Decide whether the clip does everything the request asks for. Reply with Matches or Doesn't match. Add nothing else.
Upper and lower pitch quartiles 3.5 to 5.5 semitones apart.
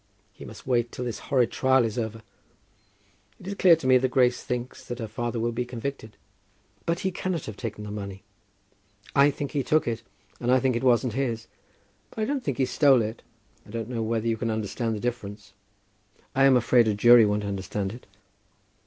Doesn't match